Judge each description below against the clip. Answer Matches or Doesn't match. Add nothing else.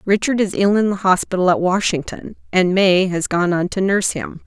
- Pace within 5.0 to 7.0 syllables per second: Matches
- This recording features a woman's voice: Matches